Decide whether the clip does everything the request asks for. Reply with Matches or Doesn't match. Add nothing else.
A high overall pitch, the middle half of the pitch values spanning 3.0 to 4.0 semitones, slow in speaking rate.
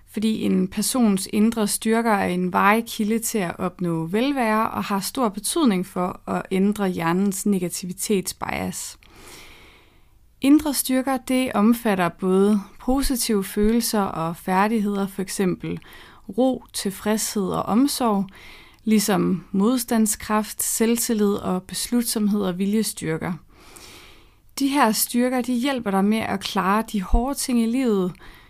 Matches